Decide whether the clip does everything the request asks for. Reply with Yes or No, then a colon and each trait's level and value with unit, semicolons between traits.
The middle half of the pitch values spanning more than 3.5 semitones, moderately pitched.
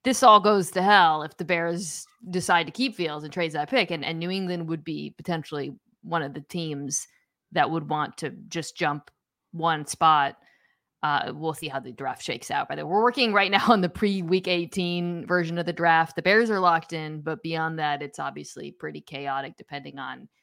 No: average, 3.1 semitones; medium, 170 Hz